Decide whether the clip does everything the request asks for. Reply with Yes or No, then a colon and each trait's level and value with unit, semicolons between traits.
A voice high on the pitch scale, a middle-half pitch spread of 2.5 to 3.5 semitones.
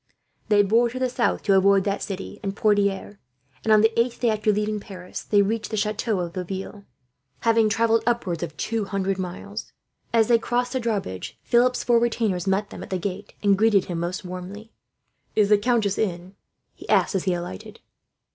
Yes: high, 205 Hz; average, 2.9 semitones